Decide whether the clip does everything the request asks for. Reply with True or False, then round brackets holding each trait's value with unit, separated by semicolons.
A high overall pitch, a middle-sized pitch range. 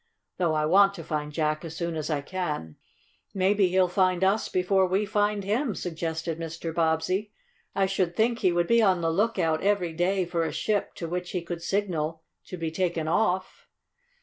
False (180 Hz; 3.1 semitones)